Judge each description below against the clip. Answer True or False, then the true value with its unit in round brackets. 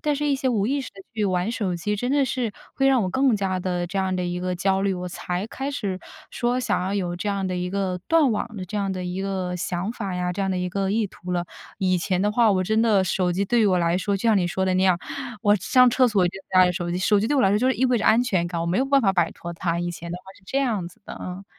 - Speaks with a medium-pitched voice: False (195 Hz)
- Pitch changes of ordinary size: True (3.7 semitones)